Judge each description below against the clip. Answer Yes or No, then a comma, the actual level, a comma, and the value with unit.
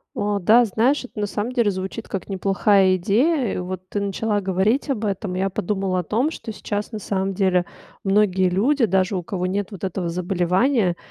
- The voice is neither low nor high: No, high, 195 Hz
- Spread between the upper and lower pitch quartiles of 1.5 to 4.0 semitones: Yes, average, 2.7 semitones